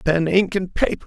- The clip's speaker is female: No, male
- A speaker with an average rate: No, fast, 225 wpm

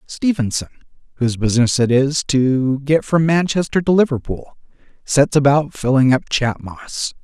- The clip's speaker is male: Yes, male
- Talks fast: No, average, 140 wpm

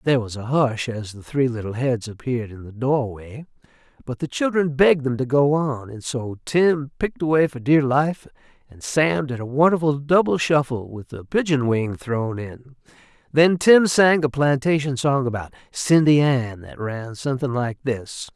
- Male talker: Yes, male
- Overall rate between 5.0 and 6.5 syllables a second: No, 4.7 syllables/s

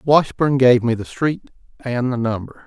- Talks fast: No, average, 155 wpm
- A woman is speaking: No, male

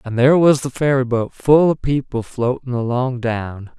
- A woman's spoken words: No, male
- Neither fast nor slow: Yes, average, 175 wpm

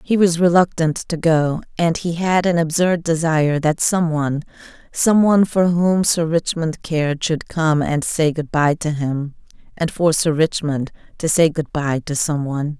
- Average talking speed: Yes, average, 175 wpm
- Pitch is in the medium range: Yes, medium, 160 Hz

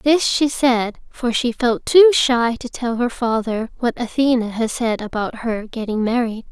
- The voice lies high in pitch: Yes, high, 240 Hz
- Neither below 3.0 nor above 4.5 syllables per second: Yes, 4.3 syllables/s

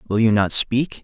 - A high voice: No, low, 115 Hz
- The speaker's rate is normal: No, fast, 235 wpm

